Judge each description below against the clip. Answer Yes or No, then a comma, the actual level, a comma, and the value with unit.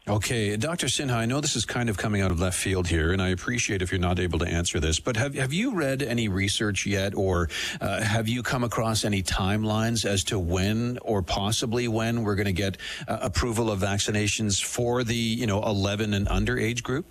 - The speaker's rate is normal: No, fast, 225 wpm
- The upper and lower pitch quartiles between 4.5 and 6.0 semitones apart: No, average, 3.4 semitones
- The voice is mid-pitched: No, low, 105 Hz